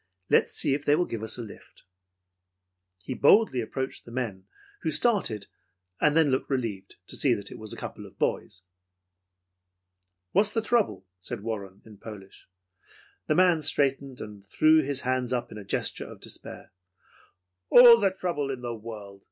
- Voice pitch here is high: No, low, 130 Hz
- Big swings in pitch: Yes, wide, 6.6 semitones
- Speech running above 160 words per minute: Yes, average, 170 wpm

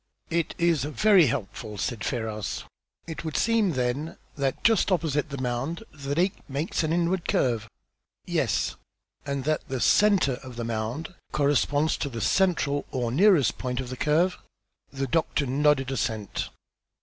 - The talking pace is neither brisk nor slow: Yes, average, 150 wpm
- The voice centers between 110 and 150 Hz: Yes, medium, 140 Hz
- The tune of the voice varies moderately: Yes, average, 4.9 semitones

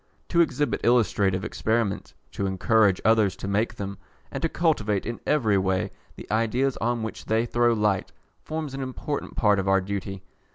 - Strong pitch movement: No, average, 3.6 semitones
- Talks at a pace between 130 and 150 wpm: No, average, 170 wpm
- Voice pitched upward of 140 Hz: No, low, 110 Hz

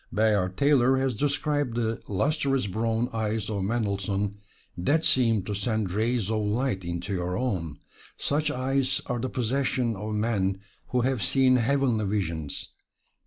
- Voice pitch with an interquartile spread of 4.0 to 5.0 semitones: Yes, average, 4.4 semitones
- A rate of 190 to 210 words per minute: No, average, 145 wpm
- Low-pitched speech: Yes, low, 110 Hz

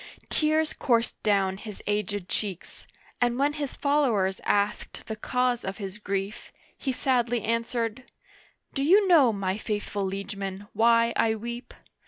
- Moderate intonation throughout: Yes, average, 3.9 semitones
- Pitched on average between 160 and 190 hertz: No, high, 225 Hz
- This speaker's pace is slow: No, average, 145 wpm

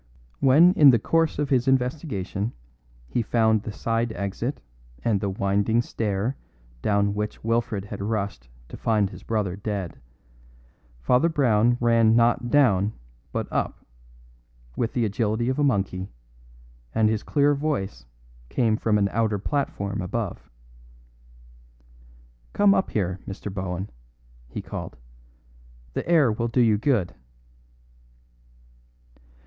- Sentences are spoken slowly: Yes, slow, 125 wpm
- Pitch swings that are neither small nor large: Yes, average, 3.8 semitones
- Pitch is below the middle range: Yes, low, 110 Hz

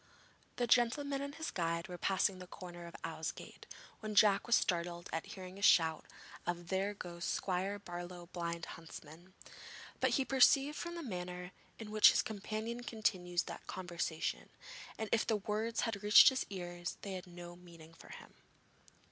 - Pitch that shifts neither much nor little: Yes, average, 3.9 semitones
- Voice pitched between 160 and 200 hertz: Yes, medium, 185 Hz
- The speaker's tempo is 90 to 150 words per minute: No, average, 165 wpm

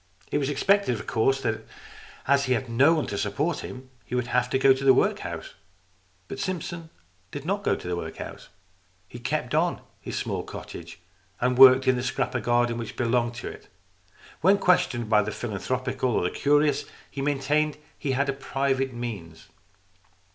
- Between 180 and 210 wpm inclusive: Yes, average, 185 wpm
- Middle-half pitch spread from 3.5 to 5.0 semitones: No, average, 3.1 semitones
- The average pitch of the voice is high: No, low, 130 Hz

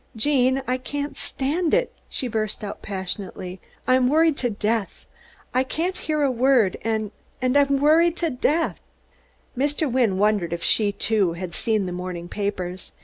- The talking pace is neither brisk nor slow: Yes, average, 155 wpm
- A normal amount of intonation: No, wide, 6.1 semitones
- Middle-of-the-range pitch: No, high, 245 Hz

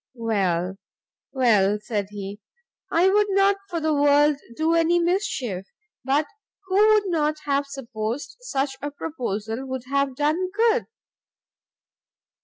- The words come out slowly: Yes, slow, 125 wpm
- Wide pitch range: Yes, wide, 7.3 semitones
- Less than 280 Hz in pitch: No, very high, 285 Hz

